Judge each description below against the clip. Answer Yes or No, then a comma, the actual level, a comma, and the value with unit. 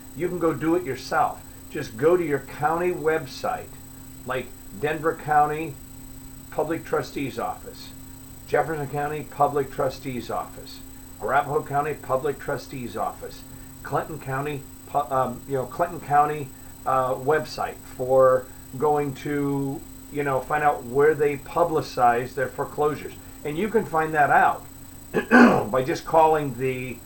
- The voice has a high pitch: No, medium, 140 Hz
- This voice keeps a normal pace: No, slow, 130 wpm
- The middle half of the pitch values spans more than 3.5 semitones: No, narrow, 2.5 semitones